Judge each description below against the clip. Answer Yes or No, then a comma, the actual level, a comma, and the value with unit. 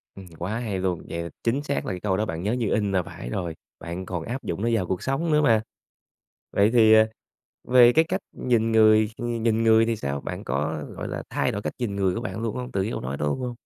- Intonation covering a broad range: No, average, 4.3 semitones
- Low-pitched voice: Yes, low, 110 Hz